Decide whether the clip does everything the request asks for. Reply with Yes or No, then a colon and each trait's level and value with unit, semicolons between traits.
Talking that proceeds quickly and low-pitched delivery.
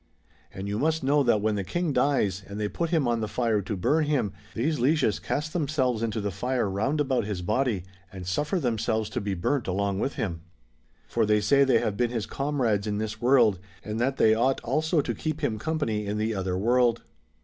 Yes: fast, 220 wpm; low, 115 Hz